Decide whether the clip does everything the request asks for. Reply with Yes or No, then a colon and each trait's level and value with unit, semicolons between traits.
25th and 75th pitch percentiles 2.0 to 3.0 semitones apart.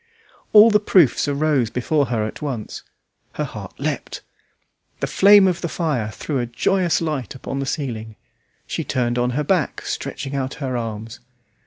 No: average, 5.2 semitones